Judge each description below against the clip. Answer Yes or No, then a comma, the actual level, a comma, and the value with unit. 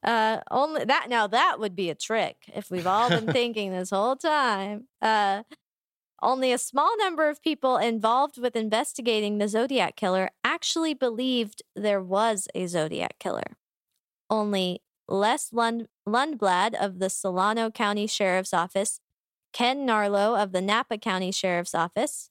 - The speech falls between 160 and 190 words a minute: No, average, 150 wpm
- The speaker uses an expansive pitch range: No, average, 4.2 semitones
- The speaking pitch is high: Yes, high, 220 Hz